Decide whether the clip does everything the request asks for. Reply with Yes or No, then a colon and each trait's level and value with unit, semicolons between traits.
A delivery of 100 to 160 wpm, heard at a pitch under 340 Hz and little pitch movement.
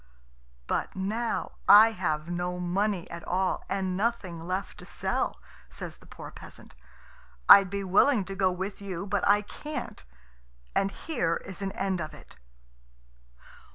Yes: average, 155 wpm; high, 190 Hz; narrow, 2.2 semitones